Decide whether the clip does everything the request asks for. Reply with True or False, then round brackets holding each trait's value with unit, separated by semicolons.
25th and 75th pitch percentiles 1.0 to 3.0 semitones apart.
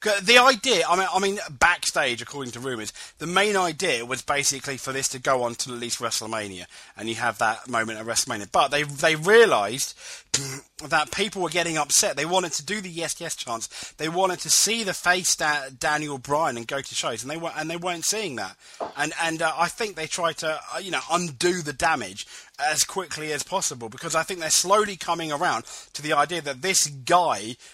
False (4.8 semitones)